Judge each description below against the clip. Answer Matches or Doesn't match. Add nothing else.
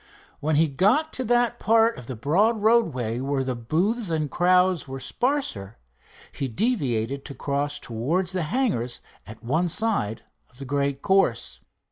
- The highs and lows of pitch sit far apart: Matches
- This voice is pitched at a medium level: Matches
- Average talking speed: Matches